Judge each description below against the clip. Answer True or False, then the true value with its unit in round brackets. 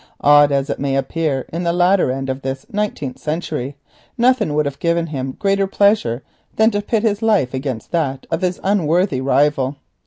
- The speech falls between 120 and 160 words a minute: False (185 wpm)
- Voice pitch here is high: False (150 Hz)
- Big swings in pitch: True (6.4 semitones)